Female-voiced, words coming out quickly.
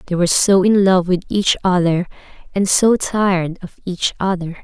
No: female; average, 170 wpm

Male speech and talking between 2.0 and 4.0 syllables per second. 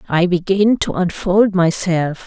No: female; 3.8 syllables/s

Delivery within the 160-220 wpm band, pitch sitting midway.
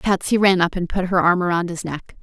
No: fast, 270 wpm; medium, 180 Hz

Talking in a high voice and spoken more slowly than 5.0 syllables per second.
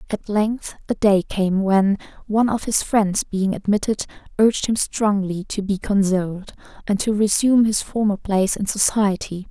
Yes: high, 205 Hz; 4.8 syllables/s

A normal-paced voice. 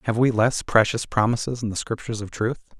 No: fast, 215 wpm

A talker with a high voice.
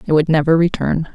No: medium, 160 Hz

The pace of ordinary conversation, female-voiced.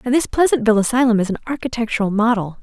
Yes: average, 185 wpm; female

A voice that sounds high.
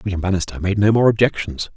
No: low, 100 Hz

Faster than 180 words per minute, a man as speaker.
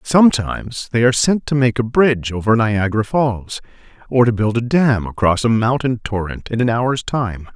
Yes: average, 190 wpm; male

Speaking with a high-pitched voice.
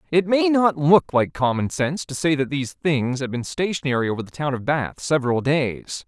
No: medium, 145 Hz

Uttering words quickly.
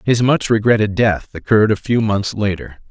No: average, 185 wpm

